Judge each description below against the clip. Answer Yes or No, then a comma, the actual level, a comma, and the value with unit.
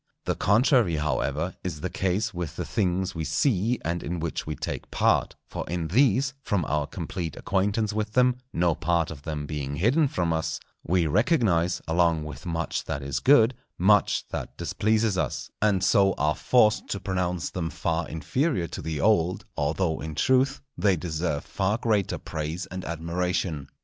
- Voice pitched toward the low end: Yes, very low, 90 Hz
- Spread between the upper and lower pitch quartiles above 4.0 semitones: Yes, average, 4.7 semitones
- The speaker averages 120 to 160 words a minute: No, average, 170 wpm